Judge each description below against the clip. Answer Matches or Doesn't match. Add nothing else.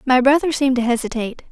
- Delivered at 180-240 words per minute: Matches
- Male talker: Doesn't match